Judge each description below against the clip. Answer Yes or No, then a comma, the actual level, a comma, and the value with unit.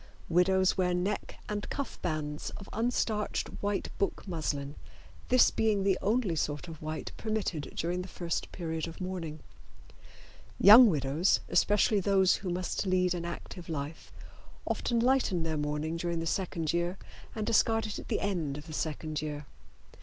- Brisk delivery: No, average, 160 wpm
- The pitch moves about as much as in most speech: Yes, average, 4.2 semitones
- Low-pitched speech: No, medium, 180 Hz